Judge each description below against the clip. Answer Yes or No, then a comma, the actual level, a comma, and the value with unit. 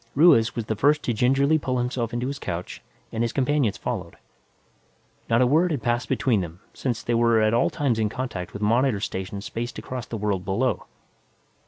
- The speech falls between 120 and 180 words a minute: No, average, 195 wpm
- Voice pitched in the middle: No, low, 120 Hz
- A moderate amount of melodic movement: Yes, average, 3.4 semitones